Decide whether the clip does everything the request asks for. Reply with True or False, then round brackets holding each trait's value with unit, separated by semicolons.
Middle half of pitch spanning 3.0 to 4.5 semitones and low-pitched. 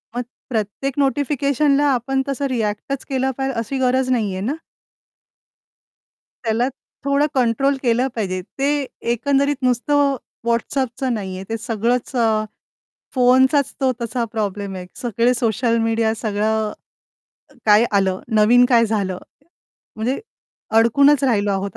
False (3.6 semitones; 240 Hz)